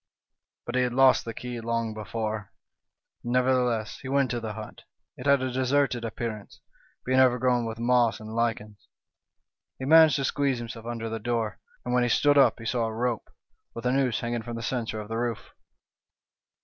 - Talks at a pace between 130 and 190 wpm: No, average, 200 wpm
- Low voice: Yes, low, 120 Hz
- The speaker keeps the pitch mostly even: Yes, narrow, 2.0 semitones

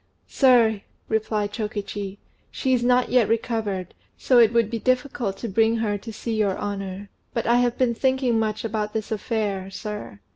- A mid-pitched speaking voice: No, high, 220 Hz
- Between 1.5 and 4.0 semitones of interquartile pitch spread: Yes, narrow, 2.6 semitones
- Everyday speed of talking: Yes, average, 175 wpm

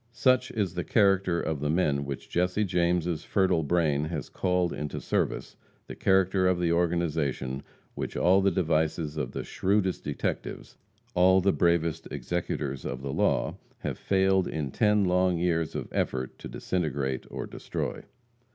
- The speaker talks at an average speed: Yes, average, 155 wpm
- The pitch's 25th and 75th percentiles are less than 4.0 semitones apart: Yes, average, 3.5 semitones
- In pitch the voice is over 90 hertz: No, very low, 85 Hz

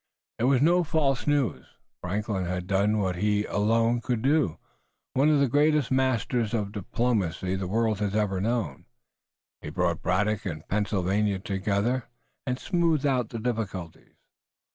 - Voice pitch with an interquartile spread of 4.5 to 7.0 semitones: Yes, average, 4.8 semitones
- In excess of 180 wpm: No, average, 145 wpm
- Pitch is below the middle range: Yes, low, 110 Hz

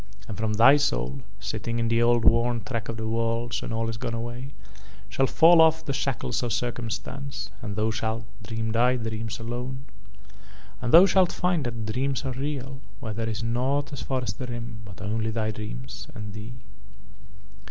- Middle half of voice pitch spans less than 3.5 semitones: Yes, average, 2.8 semitones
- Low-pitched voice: Yes, low, 115 Hz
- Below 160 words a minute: No, average, 185 wpm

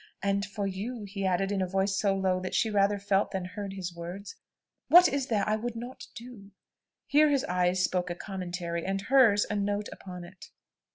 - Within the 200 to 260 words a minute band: Yes, fast, 205 wpm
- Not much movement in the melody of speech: Yes, narrow, 2.3 semitones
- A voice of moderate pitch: No, high, 195 Hz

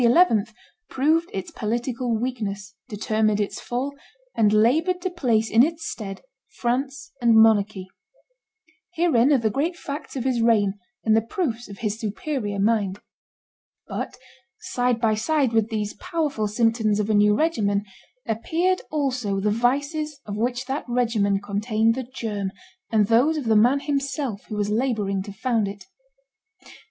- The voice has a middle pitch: No, high, 230 Hz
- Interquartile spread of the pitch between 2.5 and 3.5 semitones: No, average, 4.3 semitones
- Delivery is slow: No, average, 150 wpm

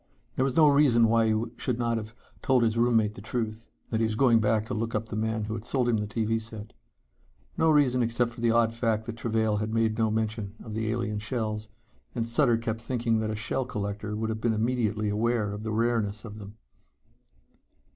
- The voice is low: Yes, low, 110 Hz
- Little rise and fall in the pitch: Yes, narrow, 1.5 semitones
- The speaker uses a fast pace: Yes, fast, 215 wpm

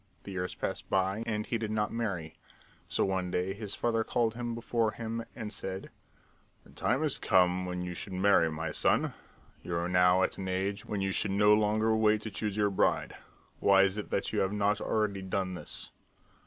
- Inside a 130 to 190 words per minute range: No, fast, 205 wpm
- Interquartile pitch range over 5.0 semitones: No, average, 2.7 semitones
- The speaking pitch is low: Yes, low, 100 Hz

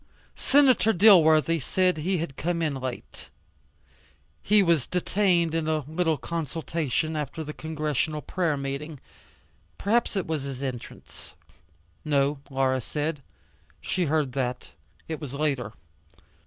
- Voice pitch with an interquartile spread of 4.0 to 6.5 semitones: No, average, 3.4 semitones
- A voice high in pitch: No, medium, 155 Hz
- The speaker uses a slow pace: Yes, slow, 125 wpm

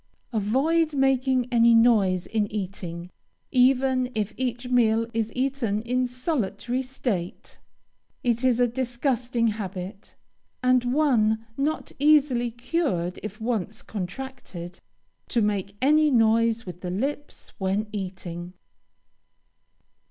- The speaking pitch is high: Yes, high, 235 Hz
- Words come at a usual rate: No, slow, 110 wpm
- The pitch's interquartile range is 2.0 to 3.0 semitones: No, average, 4.1 semitones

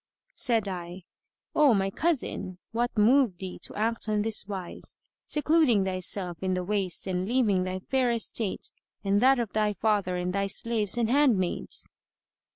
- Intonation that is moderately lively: Yes, average, 4.1 semitones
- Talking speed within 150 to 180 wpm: Yes, average, 160 wpm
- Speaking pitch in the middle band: No, high, 210 Hz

